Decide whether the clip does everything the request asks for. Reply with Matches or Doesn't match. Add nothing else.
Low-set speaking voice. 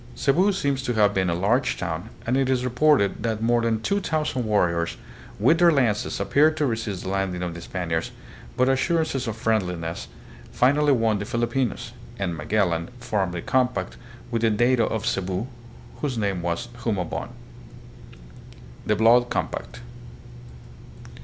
Matches